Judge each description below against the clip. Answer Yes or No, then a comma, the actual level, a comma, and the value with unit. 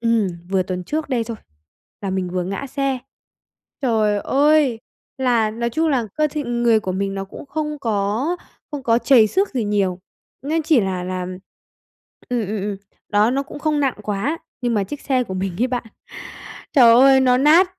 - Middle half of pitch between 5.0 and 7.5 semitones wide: Yes, wide, 5.4 semitones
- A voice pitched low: No, high, 235 Hz